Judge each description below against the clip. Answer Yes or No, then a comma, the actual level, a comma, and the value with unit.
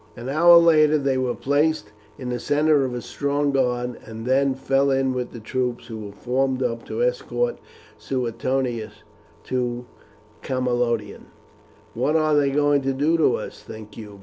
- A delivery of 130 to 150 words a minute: No, average, 165 wpm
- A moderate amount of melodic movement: Yes, average, 3.0 semitones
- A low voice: Yes, low, 130 Hz